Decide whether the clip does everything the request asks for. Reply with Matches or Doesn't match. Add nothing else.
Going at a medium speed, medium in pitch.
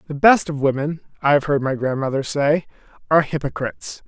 Matches